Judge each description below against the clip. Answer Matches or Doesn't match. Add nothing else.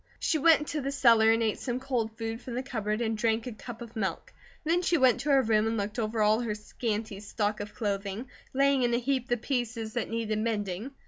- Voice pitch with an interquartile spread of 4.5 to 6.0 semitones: Doesn't match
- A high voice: Matches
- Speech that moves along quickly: Matches